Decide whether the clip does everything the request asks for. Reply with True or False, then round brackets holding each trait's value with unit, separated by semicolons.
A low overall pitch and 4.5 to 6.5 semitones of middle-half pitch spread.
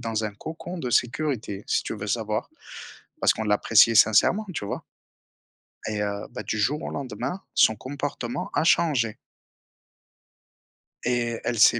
True (115 Hz; 4.9 semitones)